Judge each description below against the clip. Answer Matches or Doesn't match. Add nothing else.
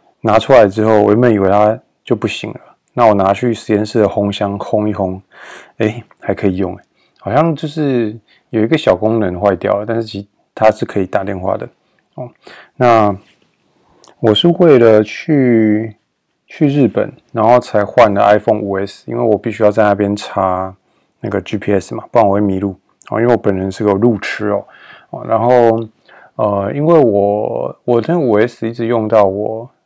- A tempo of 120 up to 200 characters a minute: Doesn't match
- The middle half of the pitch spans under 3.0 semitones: Matches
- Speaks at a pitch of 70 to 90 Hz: Doesn't match